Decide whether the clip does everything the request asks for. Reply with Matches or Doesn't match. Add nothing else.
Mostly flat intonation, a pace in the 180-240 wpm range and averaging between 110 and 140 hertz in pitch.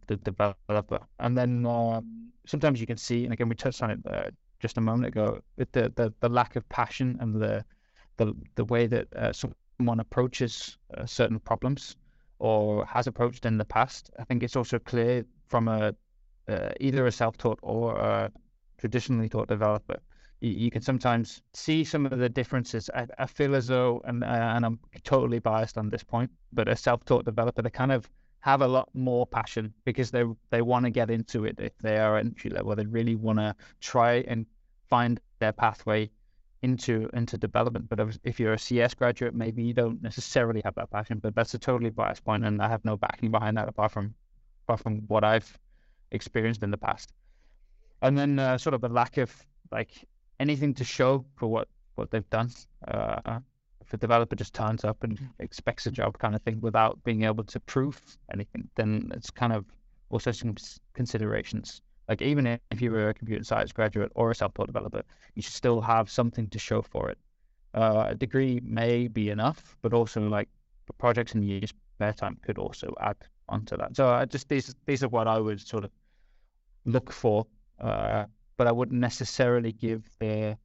Matches